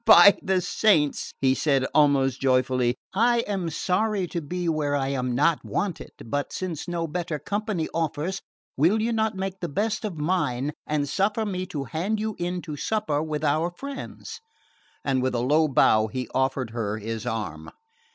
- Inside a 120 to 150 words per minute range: No, average, 175 wpm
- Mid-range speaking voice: Yes, medium, 160 Hz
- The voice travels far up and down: Yes, wide, 6.2 semitones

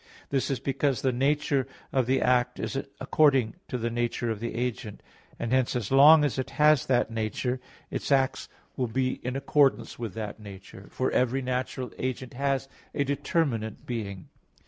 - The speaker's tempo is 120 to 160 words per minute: No, average, 170 wpm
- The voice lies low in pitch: Yes, low, 125 Hz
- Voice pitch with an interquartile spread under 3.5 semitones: Yes, narrow, 2.6 semitones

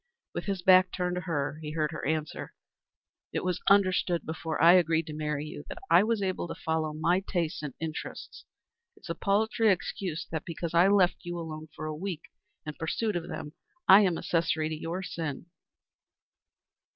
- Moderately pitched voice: Yes, medium, 170 Hz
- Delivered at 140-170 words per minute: No, average, 195 wpm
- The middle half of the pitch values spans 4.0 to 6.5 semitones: No, average, 2.9 semitones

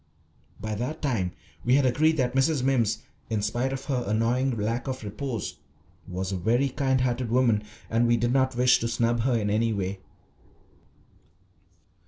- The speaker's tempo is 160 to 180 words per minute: Yes, average, 170 wpm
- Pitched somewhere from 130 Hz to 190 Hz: No, low, 120 Hz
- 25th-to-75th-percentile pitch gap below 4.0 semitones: Yes, average, 3.1 semitones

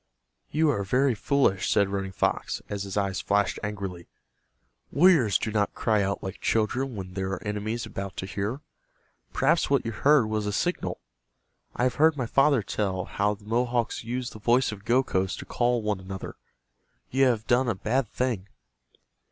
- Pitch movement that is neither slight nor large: Yes, average, 4.1 semitones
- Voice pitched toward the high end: No, low, 110 Hz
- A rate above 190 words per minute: No, average, 175 wpm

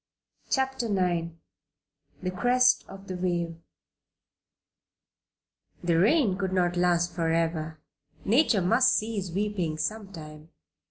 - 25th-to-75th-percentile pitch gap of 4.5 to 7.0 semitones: No, average, 4.1 semitones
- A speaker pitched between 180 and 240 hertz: Yes, medium, 185 Hz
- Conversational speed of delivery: No, slow, 105 wpm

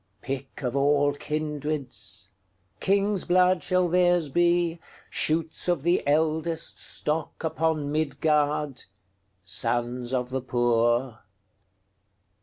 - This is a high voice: No, medium, 145 Hz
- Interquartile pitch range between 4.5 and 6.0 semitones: Yes, average, 5.2 semitones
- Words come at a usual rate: No, slow, 75 wpm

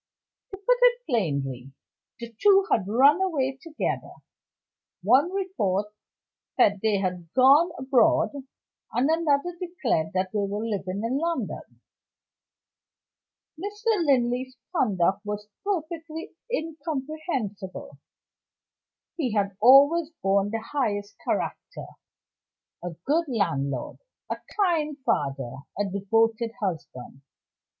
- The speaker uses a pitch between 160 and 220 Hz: No, high, 245 Hz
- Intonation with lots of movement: Yes, wide, 8.3 semitones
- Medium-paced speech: No, slow, 105 wpm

